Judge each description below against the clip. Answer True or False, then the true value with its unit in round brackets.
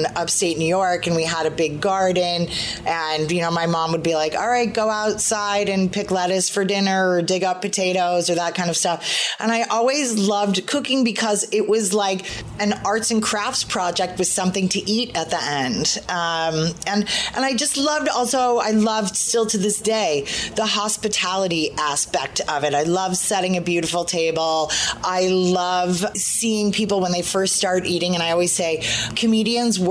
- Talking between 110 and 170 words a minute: False (190 wpm)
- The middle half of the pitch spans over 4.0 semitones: False (3.6 semitones)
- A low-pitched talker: False (190 Hz)